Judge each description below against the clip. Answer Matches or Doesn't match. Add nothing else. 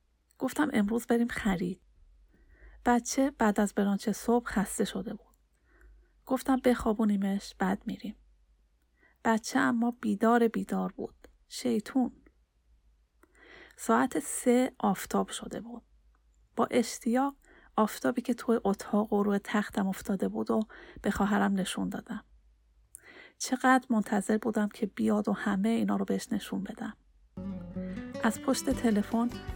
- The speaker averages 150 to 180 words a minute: Doesn't match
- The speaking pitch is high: Matches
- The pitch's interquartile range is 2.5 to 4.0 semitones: Matches